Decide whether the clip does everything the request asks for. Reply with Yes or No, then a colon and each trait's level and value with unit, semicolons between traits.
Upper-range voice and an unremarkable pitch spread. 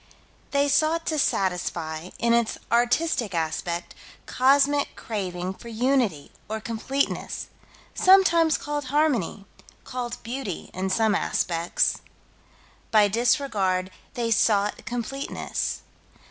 No: high, 235 Hz; wide, 6.6 semitones